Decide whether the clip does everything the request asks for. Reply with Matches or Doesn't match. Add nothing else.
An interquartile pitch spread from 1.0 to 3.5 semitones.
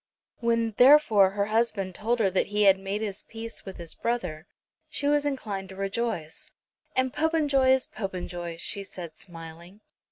Doesn't match